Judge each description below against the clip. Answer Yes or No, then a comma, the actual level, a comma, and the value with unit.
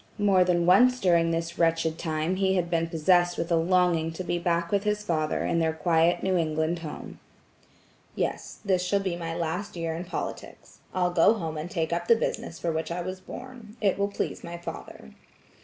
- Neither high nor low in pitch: Yes, medium, 175 Hz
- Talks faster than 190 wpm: Yes, fast, 205 wpm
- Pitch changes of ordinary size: No, narrow, 2.2 semitones